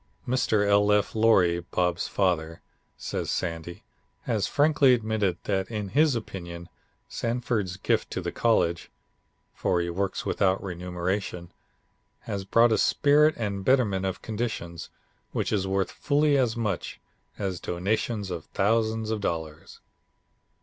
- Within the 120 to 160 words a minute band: Yes, slow, 135 wpm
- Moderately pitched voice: No, low, 100 Hz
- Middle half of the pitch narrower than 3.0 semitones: No, average, 4.3 semitones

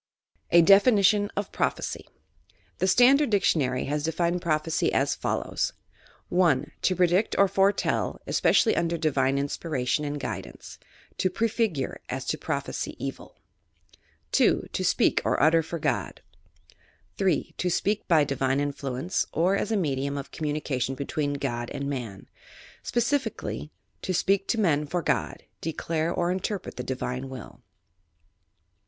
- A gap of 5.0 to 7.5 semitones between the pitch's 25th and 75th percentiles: Yes, wide, 5.4 semitones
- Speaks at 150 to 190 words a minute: No, average, 140 wpm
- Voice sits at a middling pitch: Yes, medium, 165 Hz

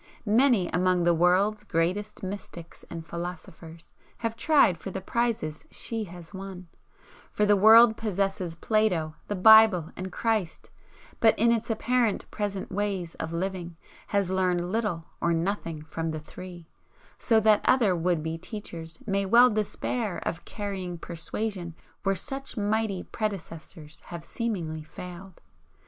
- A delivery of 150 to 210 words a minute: No, average, 140 wpm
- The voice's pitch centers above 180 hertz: Yes, high, 190 Hz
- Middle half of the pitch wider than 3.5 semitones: Yes, average, 4.1 semitones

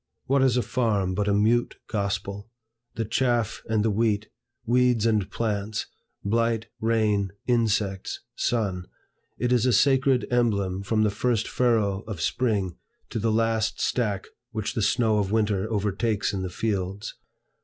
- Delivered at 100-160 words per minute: Yes, average, 150 wpm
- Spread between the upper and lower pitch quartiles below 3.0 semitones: Yes, narrow, 2.6 semitones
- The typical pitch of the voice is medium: No, low, 110 Hz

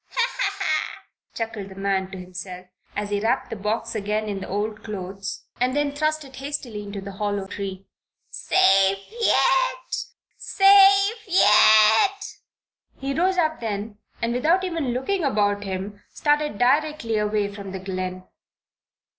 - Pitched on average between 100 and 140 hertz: No, high, 215 Hz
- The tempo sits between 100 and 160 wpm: Yes, average, 150 wpm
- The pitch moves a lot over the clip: Yes, wide, 7.0 semitones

